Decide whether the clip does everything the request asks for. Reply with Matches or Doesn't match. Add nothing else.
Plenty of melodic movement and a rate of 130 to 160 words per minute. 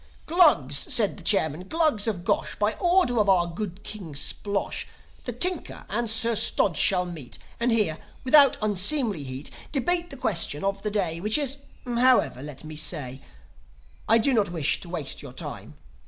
Doesn't match